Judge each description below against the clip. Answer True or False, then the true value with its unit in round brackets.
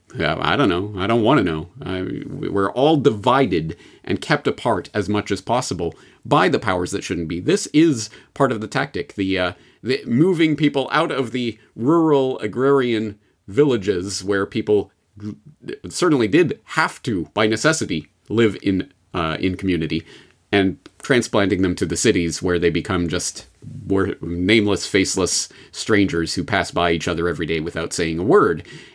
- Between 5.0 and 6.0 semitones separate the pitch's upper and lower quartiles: False (4.3 semitones)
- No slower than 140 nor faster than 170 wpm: True (160 wpm)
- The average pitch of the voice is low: True (100 Hz)